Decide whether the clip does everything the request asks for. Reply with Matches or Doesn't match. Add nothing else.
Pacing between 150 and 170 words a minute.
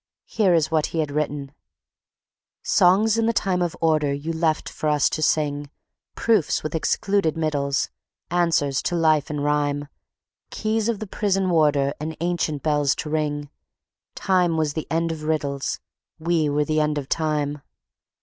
Matches